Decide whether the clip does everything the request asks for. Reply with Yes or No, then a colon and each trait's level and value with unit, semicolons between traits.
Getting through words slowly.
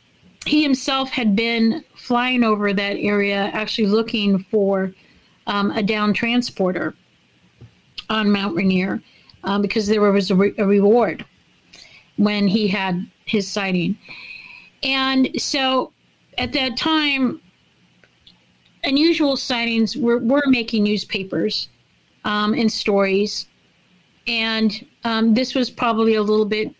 Yes: slow, 120 wpm